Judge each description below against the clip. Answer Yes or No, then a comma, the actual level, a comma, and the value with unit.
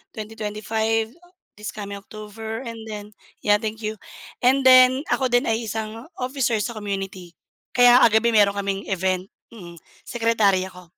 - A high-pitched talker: Yes, high, 220 Hz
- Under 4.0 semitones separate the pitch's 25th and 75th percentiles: Yes, narrow, 2.5 semitones